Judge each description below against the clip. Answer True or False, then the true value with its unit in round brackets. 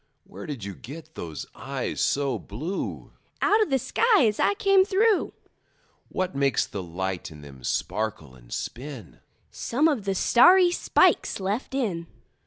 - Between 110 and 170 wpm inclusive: True (155 wpm)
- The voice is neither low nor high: True (165 Hz)